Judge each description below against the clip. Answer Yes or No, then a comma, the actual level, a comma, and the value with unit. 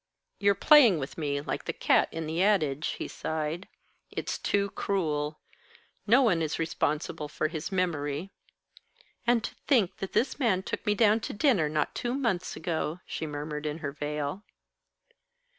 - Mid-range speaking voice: Yes, medium, 165 Hz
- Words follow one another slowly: No, average, 160 wpm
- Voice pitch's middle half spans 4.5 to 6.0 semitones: Yes, average, 5.2 semitones